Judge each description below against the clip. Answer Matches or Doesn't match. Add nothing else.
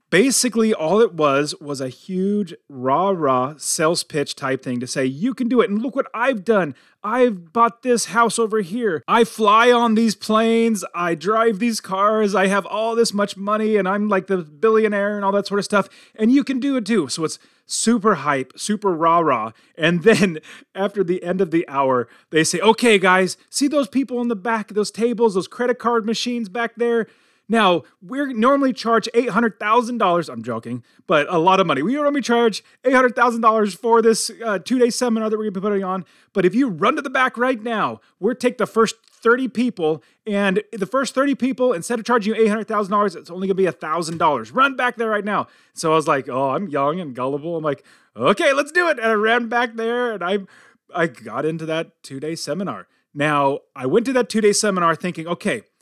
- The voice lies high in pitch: Matches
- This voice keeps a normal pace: Doesn't match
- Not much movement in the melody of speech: Doesn't match